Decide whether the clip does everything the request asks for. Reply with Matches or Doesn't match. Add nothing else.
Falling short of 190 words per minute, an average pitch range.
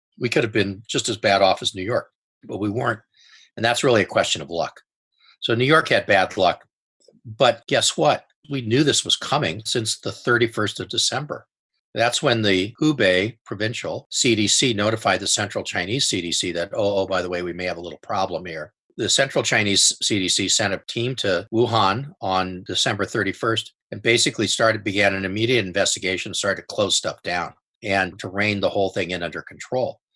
Doesn't match